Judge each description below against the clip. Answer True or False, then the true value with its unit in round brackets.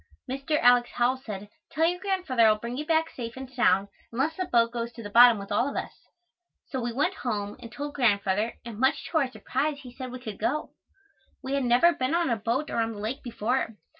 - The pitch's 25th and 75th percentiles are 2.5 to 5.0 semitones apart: True (3.6 semitones)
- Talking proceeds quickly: True (235 wpm)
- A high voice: True (245 Hz)